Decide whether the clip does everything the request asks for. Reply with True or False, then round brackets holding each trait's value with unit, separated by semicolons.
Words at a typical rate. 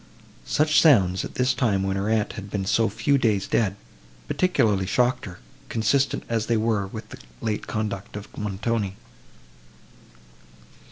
True (150 wpm)